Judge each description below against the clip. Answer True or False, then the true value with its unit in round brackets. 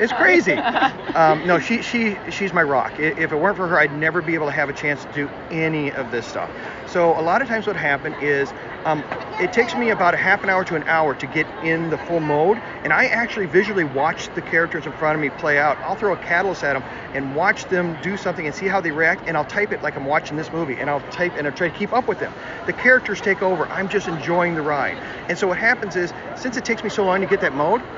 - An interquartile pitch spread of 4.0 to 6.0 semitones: True (4.3 semitones)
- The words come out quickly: True (270 wpm)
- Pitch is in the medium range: True (170 Hz)